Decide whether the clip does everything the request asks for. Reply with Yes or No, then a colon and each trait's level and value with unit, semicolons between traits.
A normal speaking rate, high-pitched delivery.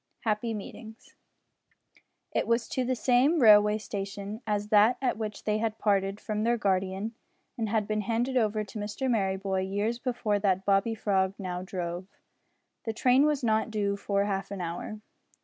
Yes: average, 165 wpm; high, 210 Hz